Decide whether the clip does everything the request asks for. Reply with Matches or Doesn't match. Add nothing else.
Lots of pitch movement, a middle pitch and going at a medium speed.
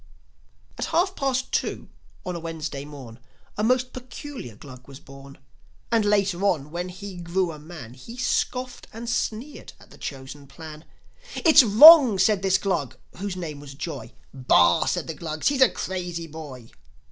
Matches